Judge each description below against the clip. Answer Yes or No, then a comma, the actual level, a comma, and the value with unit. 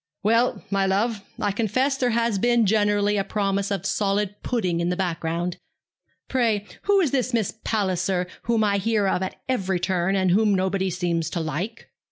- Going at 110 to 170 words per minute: No, average, 180 wpm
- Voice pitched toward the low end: No, high, 200 Hz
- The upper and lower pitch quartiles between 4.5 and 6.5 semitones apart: No, average, 3.3 semitones